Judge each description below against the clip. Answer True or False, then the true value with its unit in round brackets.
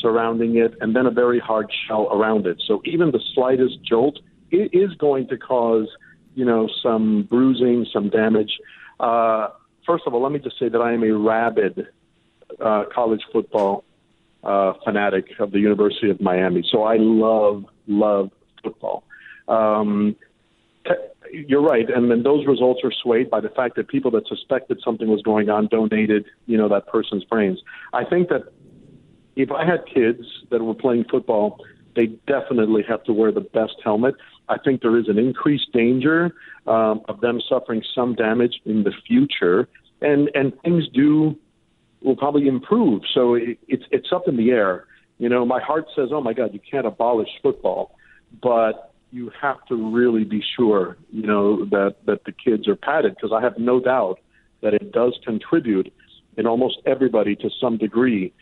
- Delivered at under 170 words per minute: False (175 wpm)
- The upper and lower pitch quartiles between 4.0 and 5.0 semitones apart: False (3.3 semitones)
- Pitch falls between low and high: False (115 Hz)